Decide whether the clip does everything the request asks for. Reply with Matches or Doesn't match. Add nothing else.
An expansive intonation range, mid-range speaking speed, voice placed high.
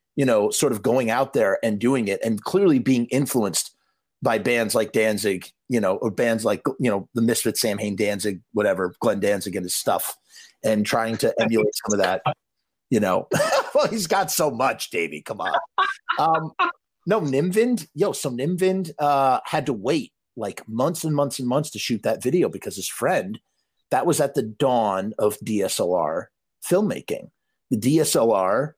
Doesn't match